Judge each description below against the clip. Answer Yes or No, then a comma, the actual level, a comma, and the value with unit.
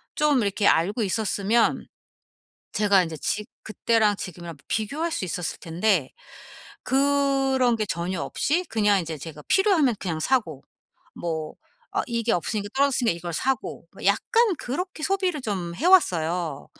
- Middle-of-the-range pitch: No, high, 215 Hz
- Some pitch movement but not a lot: No, wide, 7.8 semitones